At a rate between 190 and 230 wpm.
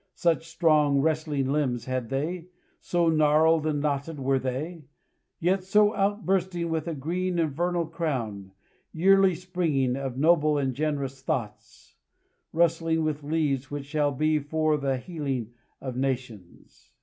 No: slow, 135 wpm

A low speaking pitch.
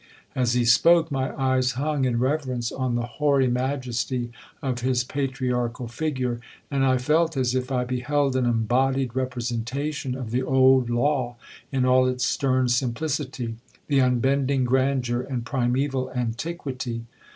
Yes: low, 130 Hz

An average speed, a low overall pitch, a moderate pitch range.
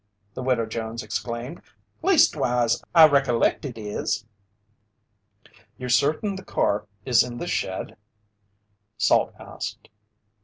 No: slow, 115 wpm; low, 125 Hz; average, 3.7 semitones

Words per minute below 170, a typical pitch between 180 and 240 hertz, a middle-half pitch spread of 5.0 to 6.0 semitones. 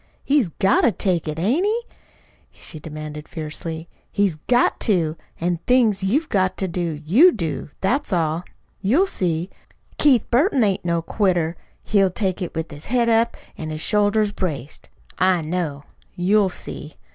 Yes: average, 155 wpm; medium, 185 Hz; average, 5.3 semitones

